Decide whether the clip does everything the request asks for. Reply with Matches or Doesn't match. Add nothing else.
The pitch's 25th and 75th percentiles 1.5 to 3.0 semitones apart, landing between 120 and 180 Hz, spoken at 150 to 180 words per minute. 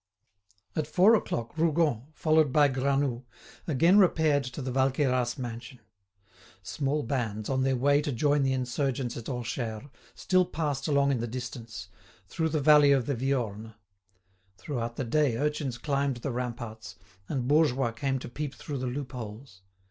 Doesn't match